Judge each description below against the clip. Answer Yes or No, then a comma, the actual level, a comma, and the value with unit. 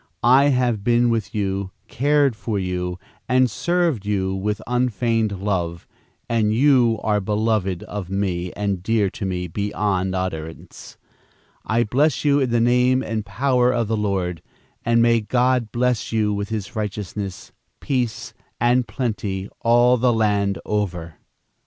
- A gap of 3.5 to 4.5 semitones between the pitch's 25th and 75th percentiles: Yes, average, 3.8 semitones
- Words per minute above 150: No, average, 145 wpm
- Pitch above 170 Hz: No, low, 110 Hz